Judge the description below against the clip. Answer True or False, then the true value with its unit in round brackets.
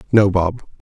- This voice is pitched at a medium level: False (100 Hz)